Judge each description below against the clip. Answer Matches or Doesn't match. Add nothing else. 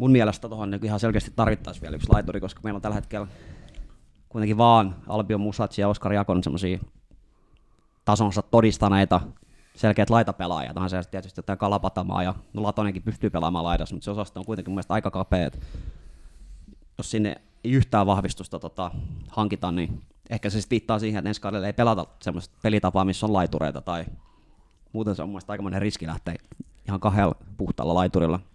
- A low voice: Matches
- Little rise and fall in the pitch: Doesn't match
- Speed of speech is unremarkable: Doesn't match